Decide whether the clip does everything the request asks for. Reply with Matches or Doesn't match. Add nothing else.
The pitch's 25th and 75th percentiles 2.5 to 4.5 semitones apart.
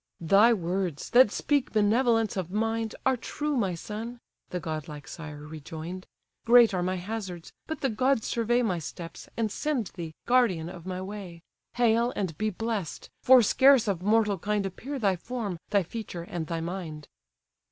Doesn't match